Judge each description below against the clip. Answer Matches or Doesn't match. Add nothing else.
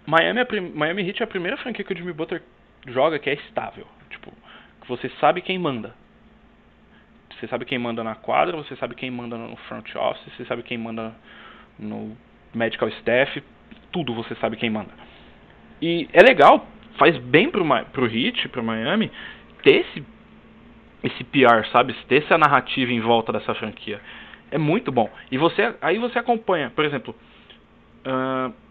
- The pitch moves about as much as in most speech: Doesn't match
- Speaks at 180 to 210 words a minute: Doesn't match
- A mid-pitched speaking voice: Doesn't match